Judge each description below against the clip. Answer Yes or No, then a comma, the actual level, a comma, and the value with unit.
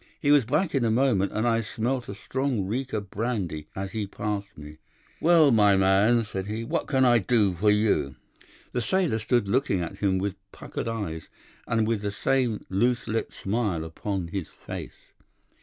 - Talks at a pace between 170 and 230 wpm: Yes, average, 185 wpm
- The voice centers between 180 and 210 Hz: No, low, 110 Hz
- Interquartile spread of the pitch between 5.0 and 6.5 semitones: No, average, 3.8 semitones